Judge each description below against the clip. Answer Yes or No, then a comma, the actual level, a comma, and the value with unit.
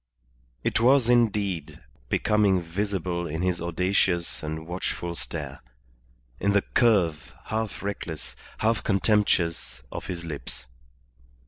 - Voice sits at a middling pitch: No, very low, 95 Hz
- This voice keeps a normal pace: No, slow, 110 wpm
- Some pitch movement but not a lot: Yes, average, 3.8 semitones